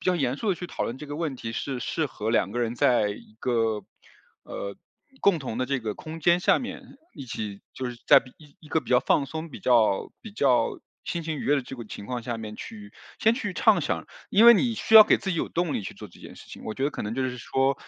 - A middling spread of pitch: No, wide, 6.3 semitones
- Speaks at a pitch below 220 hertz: Yes, low, 135 Hz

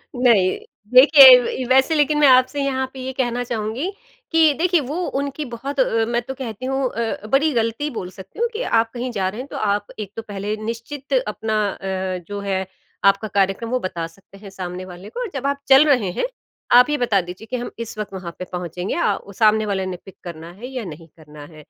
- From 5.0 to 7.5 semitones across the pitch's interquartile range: Yes, wide, 5.5 semitones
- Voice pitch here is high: Yes, high, 230 Hz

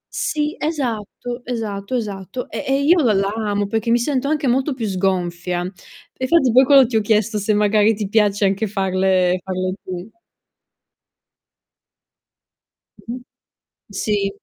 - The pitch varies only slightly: No, average, 4.3 semitones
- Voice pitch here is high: Yes, high, 215 Hz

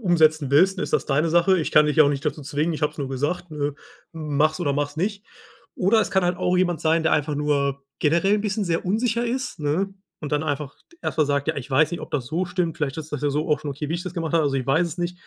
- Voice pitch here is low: No, medium, 155 Hz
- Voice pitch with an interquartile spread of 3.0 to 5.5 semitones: Yes, average, 3.5 semitones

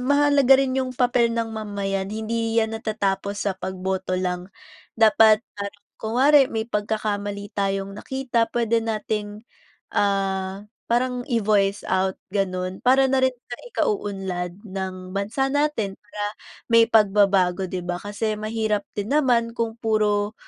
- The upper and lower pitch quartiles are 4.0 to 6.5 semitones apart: No, average, 2.9 semitones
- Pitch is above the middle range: Yes, high, 210 Hz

